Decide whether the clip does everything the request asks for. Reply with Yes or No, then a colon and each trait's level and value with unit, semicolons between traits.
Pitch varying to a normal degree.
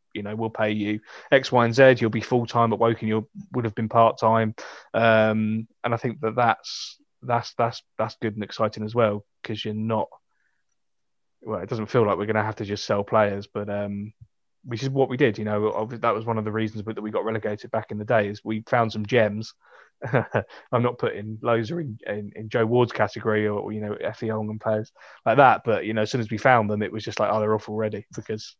No: narrow, 1.6 semitones